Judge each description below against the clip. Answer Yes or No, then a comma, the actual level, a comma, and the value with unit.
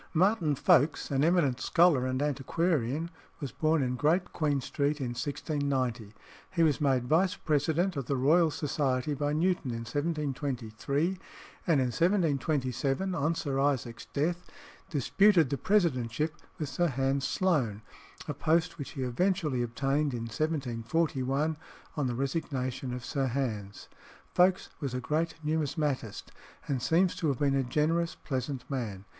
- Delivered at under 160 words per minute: Yes, average, 145 wpm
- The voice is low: No, medium, 145 Hz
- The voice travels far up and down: No, average, 3.9 semitones